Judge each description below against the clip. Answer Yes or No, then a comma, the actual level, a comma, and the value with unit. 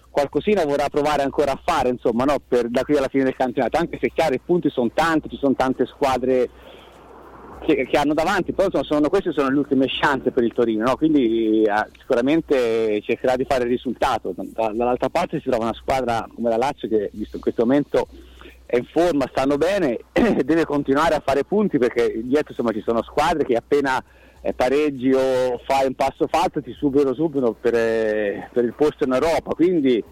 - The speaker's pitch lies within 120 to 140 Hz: Yes, low, 135 Hz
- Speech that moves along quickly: Yes, fast, 200 wpm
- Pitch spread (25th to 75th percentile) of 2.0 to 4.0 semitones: Yes, average, 3.5 semitones